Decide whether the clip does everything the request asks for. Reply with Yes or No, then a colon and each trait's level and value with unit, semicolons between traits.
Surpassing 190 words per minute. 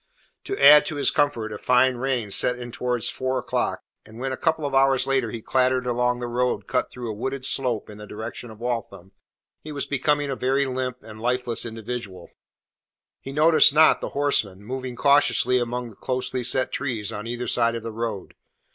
Yes: average, 200 wpm